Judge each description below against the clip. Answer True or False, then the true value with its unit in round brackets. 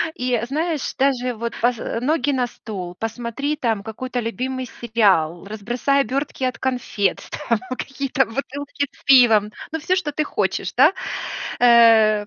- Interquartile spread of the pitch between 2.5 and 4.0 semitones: True (3.7 semitones)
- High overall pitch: True (245 Hz)